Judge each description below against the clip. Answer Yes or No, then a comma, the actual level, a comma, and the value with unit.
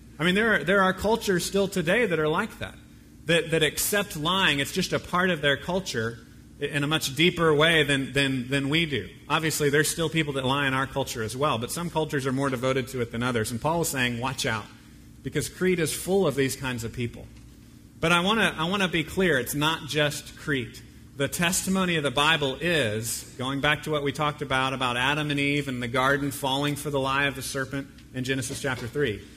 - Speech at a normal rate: No, fast, 230 wpm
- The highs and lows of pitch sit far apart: No, average, 3.5 semitones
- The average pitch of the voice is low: No, medium, 145 Hz